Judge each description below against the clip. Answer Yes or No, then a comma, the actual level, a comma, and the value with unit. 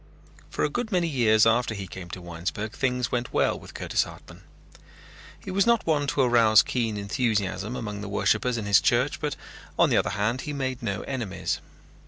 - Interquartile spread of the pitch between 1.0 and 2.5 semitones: No, average, 4.3 semitones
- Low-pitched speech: Yes, low, 115 Hz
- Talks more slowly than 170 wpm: No, average, 195 wpm